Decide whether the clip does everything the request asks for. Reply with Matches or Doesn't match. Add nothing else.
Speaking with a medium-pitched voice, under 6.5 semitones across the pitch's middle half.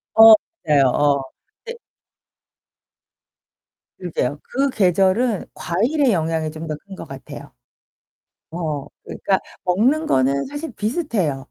Doesn't match